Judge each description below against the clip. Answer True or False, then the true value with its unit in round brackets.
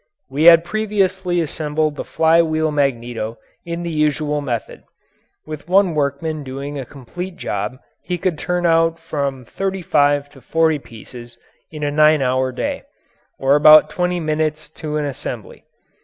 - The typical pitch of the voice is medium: True (155 Hz)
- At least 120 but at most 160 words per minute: True (155 wpm)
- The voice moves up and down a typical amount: True (3.0 semitones)